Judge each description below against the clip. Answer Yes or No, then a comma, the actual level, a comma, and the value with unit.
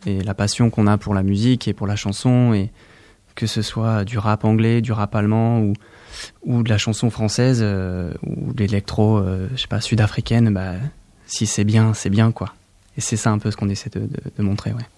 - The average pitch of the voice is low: Yes, low, 110 Hz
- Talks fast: Yes, fast, 230 wpm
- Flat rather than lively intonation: Yes, narrow, 2.3 semitones